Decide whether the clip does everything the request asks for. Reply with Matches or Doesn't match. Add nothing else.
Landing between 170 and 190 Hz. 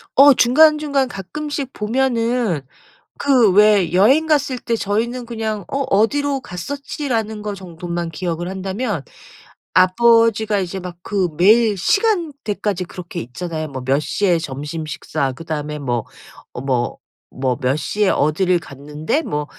Doesn't match